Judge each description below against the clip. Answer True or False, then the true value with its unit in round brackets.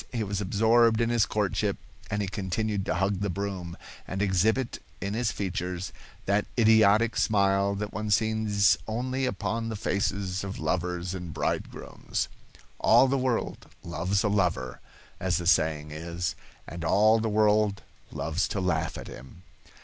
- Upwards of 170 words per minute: False (155 wpm)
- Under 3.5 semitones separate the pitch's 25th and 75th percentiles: True (3.1 semitones)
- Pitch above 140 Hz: False (100 Hz)